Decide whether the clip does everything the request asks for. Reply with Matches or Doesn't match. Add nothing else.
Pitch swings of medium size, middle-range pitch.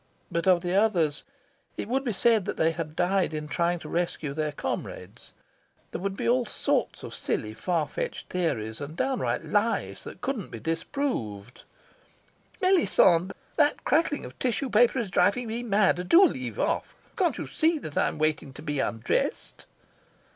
Doesn't match